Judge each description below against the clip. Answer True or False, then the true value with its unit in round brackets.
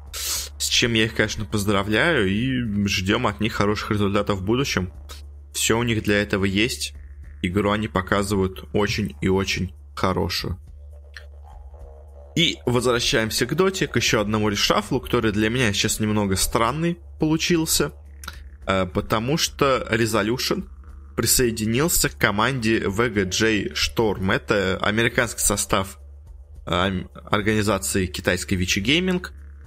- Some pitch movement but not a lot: False (6.8 semitones)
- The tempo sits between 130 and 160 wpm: False (115 wpm)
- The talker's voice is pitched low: True (105 Hz)